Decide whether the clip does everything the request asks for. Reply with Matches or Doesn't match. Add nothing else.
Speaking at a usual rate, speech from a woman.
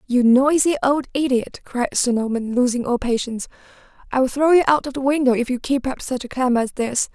Doesn't match